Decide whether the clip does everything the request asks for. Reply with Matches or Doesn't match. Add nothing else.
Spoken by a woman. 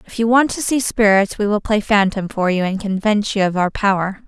Matches